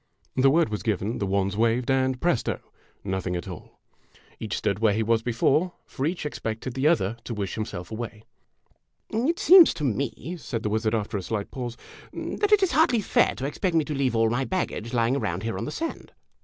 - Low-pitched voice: Yes, low, 115 Hz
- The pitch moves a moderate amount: No, wide, 5.7 semitones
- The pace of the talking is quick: Yes, fast, 210 wpm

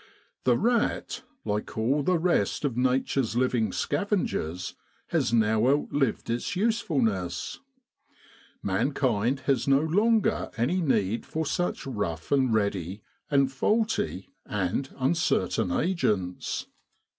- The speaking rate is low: Yes, slow, 110 wpm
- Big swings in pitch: Yes, wide, 6.9 semitones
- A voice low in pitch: Yes, low, 130 Hz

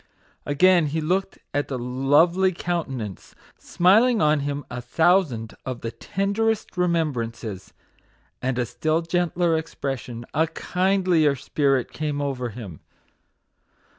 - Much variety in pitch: Yes, wide, 5.8 semitones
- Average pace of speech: No, slow, 115 wpm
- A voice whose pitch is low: No, medium, 150 Hz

